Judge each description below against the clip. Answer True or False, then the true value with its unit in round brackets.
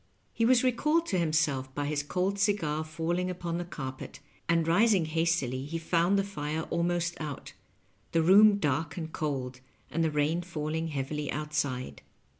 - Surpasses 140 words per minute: True (165 wpm)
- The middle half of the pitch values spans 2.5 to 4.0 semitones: True (3.1 semitones)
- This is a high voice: False (165 Hz)